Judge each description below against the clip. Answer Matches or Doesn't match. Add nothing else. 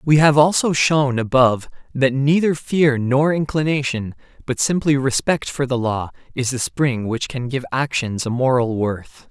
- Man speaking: Matches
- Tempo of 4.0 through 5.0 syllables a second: Matches